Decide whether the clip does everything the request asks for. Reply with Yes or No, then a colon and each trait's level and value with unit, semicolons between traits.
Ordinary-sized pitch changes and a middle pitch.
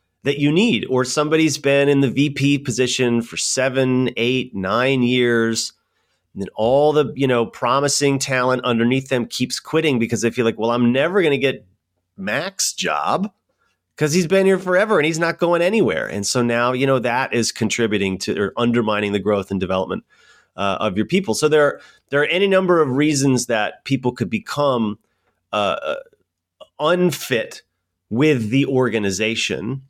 No: average, 4.0 semitones; low, 130 Hz